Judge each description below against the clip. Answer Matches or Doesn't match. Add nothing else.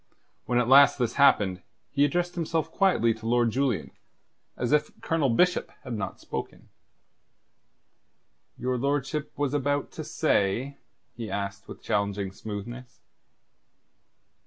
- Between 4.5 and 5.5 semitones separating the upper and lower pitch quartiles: Matches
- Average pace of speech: Doesn't match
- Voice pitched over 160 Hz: Doesn't match